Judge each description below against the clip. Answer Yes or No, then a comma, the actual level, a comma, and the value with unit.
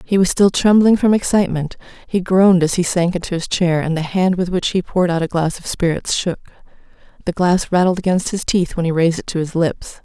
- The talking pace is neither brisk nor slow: No, fast, 240 wpm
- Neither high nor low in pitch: Yes, medium, 180 Hz